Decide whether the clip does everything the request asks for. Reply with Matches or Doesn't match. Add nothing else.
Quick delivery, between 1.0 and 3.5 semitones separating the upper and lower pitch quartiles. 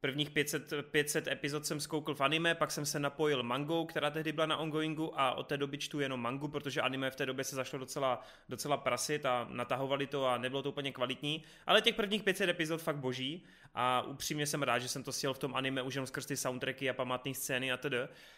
Matches